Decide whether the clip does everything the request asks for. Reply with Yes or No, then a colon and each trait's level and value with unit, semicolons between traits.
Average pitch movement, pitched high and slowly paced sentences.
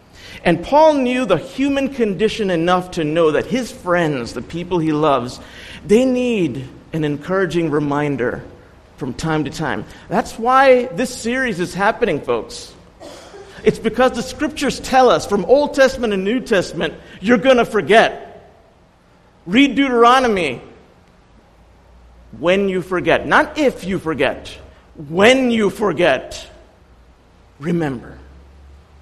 No: wide, 8.2 semitones; high, 195 Hz; slow, 125 wpm